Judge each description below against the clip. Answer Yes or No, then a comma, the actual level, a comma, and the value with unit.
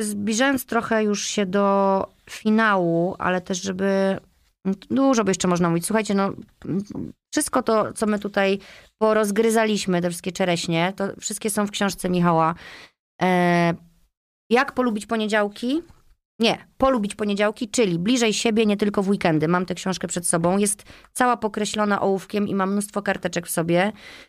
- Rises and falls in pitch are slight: No, average, 3.0 semitones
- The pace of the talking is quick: No, average, 145 wpm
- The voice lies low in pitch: No, high, 200 Hz